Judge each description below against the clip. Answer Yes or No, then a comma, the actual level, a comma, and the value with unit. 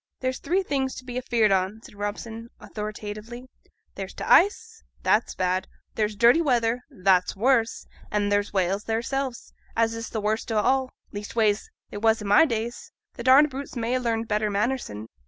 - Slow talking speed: No, average, 175 wpm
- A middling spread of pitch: Yes, average, 3.6 semitones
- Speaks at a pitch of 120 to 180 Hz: No, high, 225 Hz